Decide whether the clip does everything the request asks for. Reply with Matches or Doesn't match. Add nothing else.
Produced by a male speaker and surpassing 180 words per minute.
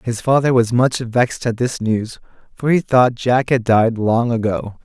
Matches